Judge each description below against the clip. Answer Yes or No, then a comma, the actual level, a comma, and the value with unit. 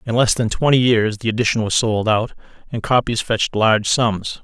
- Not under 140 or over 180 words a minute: No, fast, 205 wpm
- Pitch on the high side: No, low, 115 Hz